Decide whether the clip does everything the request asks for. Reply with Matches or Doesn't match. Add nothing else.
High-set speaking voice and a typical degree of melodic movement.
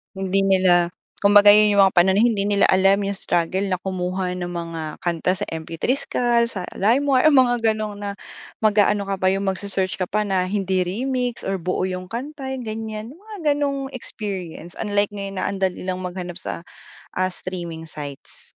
Matches